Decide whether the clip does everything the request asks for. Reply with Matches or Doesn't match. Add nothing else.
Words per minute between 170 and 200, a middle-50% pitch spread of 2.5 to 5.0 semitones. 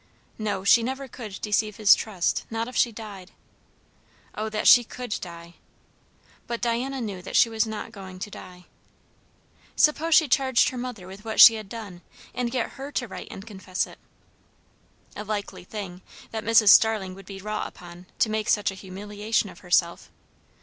Matches